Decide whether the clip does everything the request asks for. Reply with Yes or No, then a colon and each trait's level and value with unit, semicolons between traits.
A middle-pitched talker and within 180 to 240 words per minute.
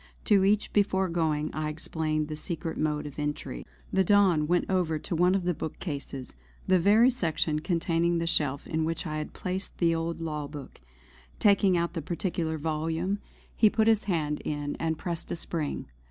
Yes: medium, 165 Hz; average, 185 wpm